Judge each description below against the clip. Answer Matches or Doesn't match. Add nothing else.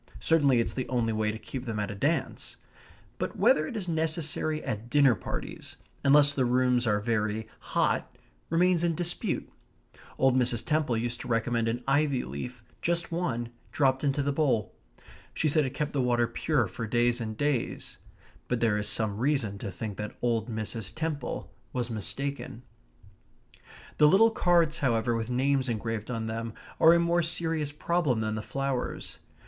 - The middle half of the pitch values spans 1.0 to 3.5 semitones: Doesn't match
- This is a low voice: Matches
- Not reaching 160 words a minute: Doesn't match